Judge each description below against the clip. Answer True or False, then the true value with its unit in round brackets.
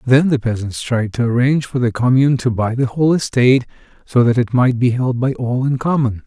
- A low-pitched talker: True (125 Hz)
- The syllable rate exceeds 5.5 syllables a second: True (5.7 syllables/s)